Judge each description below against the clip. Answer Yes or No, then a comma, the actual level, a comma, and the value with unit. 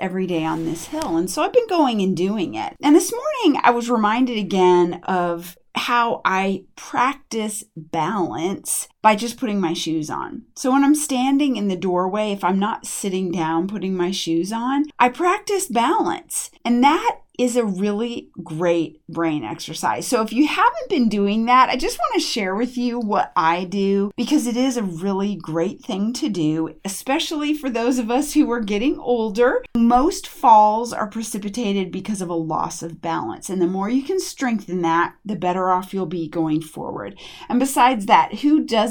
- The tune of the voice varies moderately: No, wide, 6.1 semitones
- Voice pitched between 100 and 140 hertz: No, high, 215 Hz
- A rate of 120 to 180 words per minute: No, average, 190 wpm